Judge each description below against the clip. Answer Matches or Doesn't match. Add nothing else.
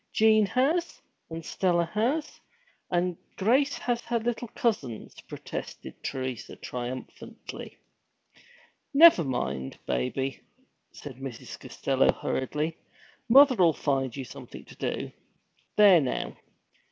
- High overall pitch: Doesn't match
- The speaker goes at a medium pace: Doesn't match